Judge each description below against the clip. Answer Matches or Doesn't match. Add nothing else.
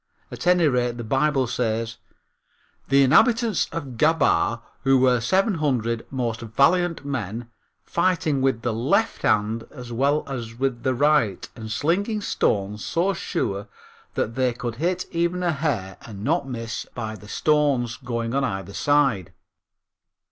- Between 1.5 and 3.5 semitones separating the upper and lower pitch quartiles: Doesn't match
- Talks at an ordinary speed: Matches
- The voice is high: Doesn't match